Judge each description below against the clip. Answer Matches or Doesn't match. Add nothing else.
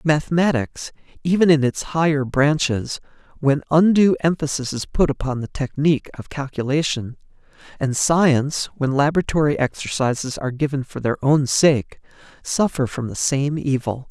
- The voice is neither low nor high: Matches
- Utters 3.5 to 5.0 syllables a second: Matches